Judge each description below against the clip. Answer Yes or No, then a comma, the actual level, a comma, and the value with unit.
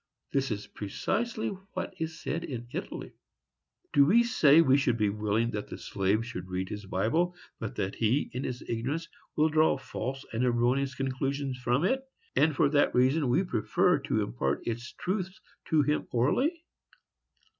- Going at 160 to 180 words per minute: Yes, average, 165 wpm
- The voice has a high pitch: No, low, 130 Hz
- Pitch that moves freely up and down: Yes, wide, 5.7 semitones